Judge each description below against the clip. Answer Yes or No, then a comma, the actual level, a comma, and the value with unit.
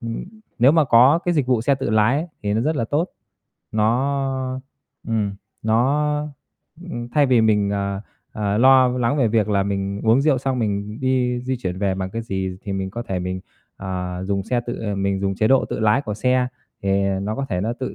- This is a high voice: No, low, 115 Hz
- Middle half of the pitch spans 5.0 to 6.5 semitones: No, average, 4.6 semitones